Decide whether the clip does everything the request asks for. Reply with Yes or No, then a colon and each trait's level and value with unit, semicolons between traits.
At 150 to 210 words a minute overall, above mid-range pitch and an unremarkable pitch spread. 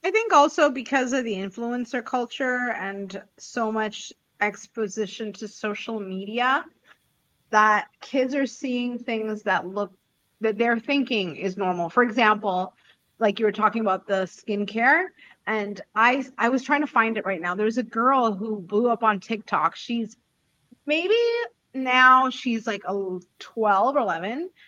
Yes: average, 155 wpm; high, 225 Hz; average, 3.8 semitones